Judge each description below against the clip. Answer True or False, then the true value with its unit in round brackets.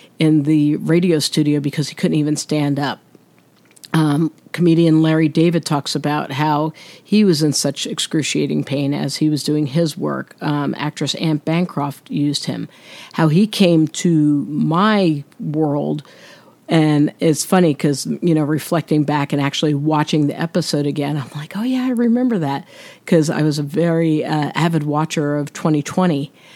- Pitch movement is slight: True (2.2 semitones)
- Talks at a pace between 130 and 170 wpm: True (165 wpm)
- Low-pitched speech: False (155 Hz)